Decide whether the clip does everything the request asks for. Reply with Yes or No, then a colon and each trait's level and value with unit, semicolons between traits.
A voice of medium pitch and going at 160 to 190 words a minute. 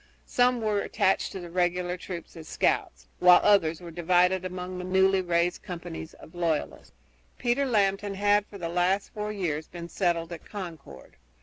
Yes: medium, 180 Hz; average, 170 wpm